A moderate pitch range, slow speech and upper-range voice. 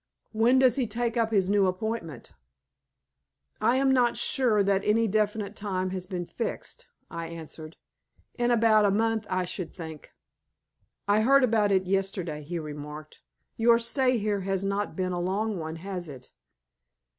No: average, 3.9 semitones; average, 160 wpm; high, 200 Hz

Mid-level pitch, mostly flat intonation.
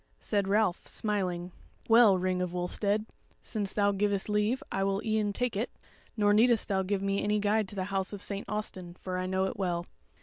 No: high, 200 Hz; narrow, 1.9 semitones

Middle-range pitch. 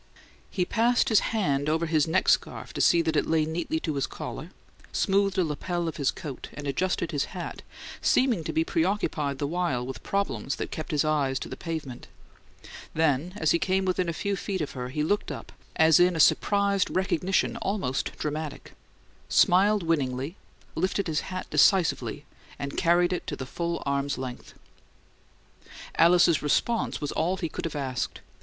Yes: medium, 165 Hz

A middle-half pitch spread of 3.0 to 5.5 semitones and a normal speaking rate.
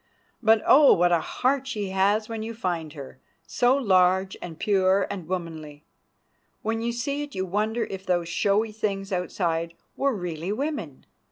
Yes: average, 4.3 semitones; average, 160 wpm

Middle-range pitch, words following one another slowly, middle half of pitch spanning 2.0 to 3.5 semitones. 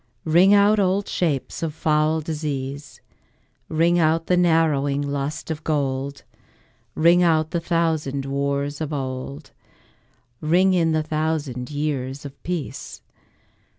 Yes: medium, 155 Hz; slow, 120 wpm; average, 2.8 semitones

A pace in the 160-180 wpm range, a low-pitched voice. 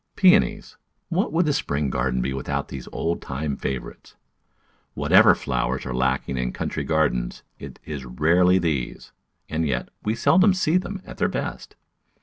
Yes: average, 165 wpm; very low, 75 Hz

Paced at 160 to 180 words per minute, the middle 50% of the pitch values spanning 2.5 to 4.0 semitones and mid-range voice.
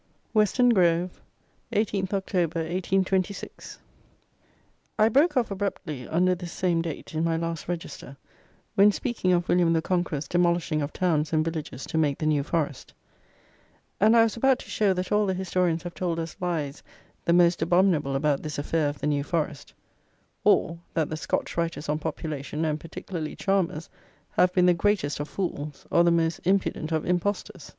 Yes: average, 170 wpm; average, 3.2 semitones; medium, 170 Hz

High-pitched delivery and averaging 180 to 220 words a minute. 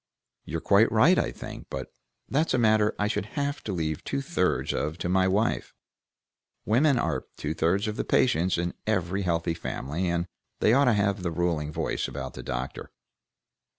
No: very low, 95 Hz; average, 185 wpm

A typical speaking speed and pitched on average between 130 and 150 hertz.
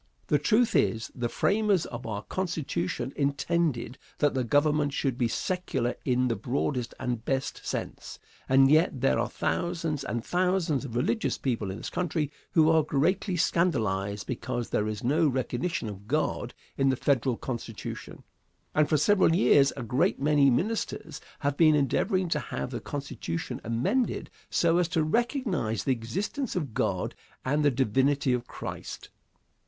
Yes: average, 160 wpm; medium, 140 Hz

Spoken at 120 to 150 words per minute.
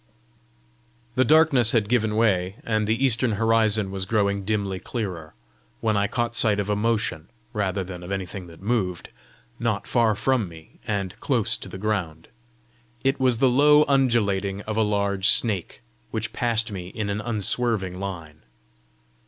No: average, 160 wpm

